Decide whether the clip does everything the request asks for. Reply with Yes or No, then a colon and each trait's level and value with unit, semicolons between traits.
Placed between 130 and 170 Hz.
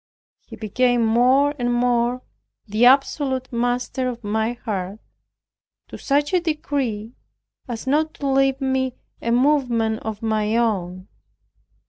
No: high, 245 Hz